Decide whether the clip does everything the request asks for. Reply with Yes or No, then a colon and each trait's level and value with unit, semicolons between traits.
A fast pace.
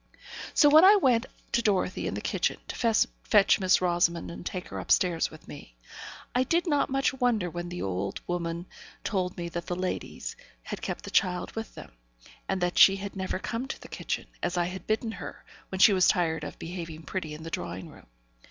Yes: fast, 210 wpm